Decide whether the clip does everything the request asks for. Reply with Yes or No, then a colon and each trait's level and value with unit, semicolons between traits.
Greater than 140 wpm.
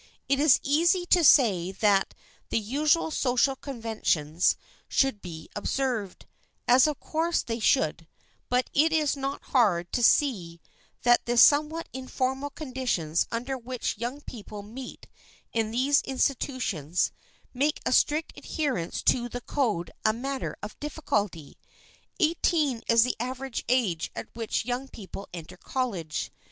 No: slow, 135 wpm